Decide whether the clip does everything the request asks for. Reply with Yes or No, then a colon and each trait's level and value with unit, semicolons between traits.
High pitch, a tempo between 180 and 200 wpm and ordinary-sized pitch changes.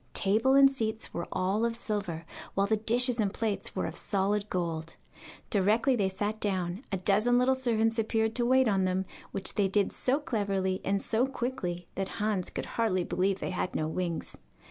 Yes: high, 205 Hz; average, 190 wpm; average, 3.4 semitones